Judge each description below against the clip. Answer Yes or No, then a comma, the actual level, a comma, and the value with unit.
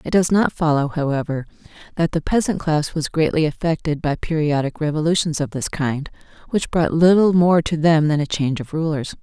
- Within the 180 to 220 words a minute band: Yes, average, 190 wpm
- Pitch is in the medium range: Yes, medium, 155 Hz